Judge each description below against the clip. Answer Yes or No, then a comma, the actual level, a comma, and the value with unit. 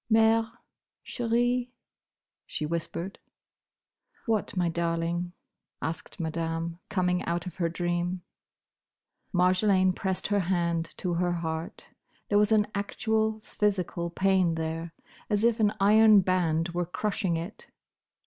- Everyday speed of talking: No, slow, 120 wpm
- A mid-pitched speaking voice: Yes, medium, 180 Hz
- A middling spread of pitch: Yes, average, 3.6 semitones